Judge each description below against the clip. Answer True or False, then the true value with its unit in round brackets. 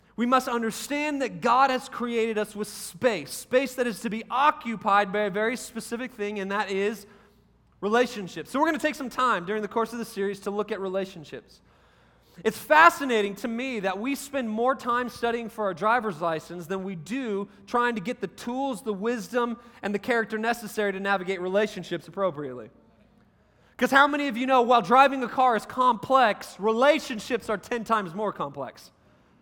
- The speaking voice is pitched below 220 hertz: False (225 Hz)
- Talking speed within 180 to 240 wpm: True (190 wpm)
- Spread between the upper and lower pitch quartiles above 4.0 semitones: False (3.7 semitones)